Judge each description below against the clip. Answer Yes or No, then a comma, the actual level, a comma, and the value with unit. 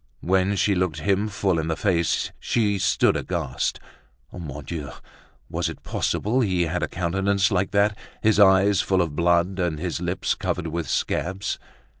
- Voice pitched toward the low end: Yes, very low, 90 Hz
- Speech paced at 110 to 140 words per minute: No, average, 165 wpm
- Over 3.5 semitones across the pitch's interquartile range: No, average, 2.7 semitones